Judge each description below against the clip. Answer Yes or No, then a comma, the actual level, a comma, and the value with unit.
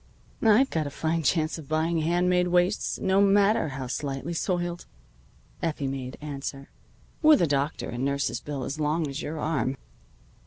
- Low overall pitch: No, medium, 155 Hz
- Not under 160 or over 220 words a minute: Yes, average, 165 wpm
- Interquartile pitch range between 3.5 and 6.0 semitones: Yes, average, 4.1 semitones